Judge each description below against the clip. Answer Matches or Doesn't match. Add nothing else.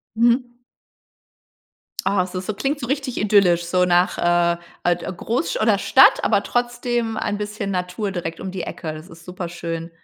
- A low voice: Doesn't match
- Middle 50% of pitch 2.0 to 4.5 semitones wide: Doesn't match